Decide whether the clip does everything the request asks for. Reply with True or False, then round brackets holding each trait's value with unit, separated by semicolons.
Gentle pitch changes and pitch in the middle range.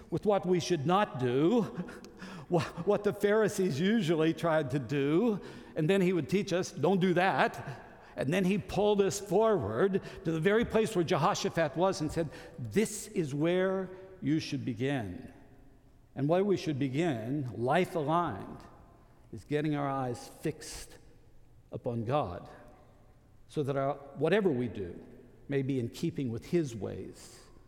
False (5.5 semitones; 160 Hz)